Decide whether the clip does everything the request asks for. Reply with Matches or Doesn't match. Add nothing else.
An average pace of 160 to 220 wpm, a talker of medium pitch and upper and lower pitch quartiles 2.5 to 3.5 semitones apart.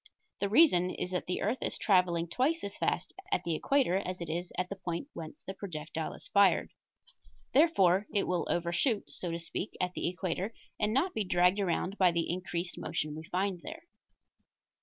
Matches